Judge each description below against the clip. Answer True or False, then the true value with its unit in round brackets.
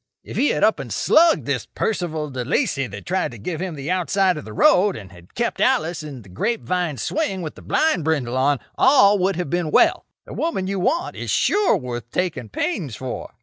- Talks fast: True (220 wpm)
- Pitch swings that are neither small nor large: False (7.2 semitones)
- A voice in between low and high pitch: True (175 Hz)